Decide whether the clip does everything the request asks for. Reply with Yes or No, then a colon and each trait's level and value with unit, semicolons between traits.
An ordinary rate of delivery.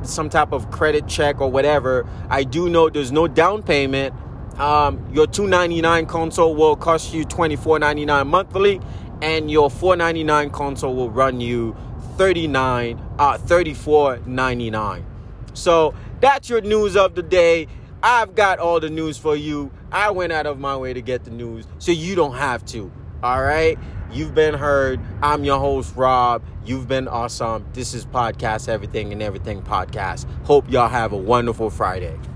Yes: average, 160 wpm